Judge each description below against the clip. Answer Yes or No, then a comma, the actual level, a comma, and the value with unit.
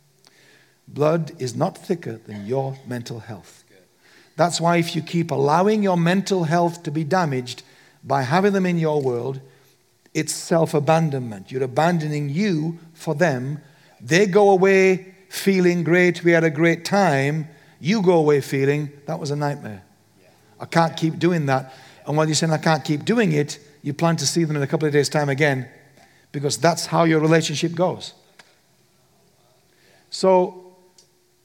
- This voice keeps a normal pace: Yes, average, 160 wpm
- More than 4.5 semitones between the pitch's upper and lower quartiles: No, average, 3.9 semitones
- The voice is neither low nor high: Yes, medium, 155 Hz